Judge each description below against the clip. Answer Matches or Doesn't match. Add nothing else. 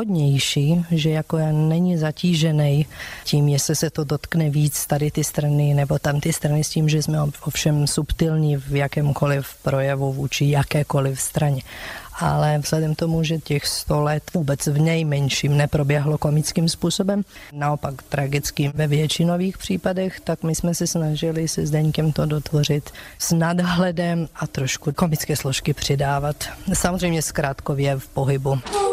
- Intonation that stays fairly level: Matches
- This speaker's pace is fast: Doesn't match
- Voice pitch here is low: Doesn't match